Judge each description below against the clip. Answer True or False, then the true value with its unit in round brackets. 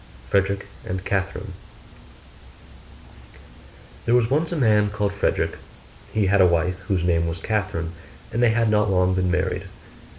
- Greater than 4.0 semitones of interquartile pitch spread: False (3.0 semitones)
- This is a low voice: True (100 Hz)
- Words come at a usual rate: True (145 wpm)